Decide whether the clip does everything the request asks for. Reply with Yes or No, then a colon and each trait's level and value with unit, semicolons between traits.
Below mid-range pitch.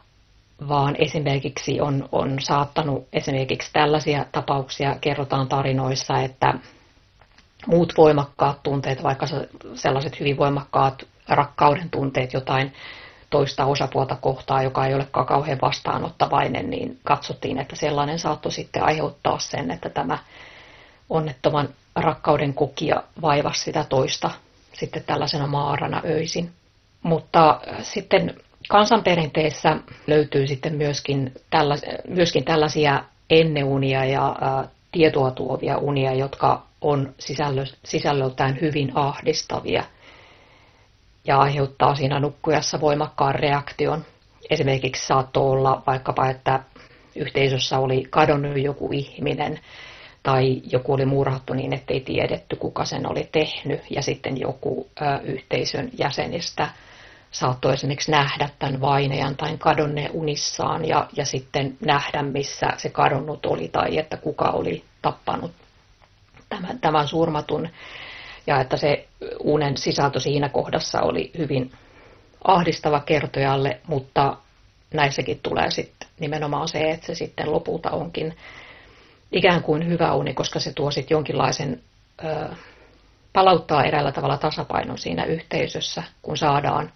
No: medium, 145 Hz